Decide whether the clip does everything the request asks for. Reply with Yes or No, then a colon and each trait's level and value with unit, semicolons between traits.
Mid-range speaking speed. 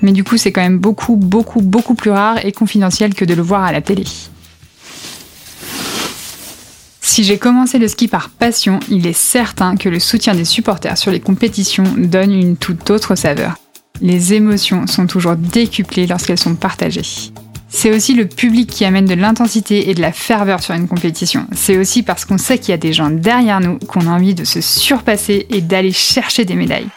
Yes: average, 200 wpm